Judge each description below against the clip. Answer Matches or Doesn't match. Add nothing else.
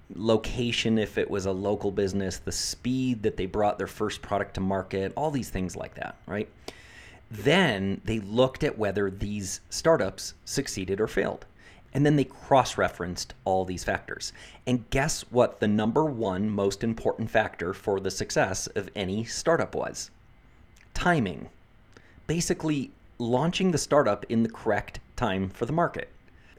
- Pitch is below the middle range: Matches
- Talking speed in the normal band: Matches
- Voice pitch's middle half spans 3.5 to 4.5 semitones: Matches